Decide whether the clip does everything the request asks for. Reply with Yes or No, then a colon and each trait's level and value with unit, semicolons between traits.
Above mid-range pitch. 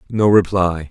No: very low, 95 Hz